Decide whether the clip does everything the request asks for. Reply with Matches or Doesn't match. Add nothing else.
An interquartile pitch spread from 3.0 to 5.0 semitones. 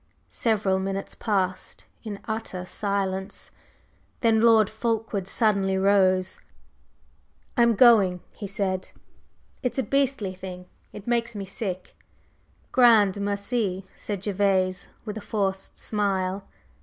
Doesn't match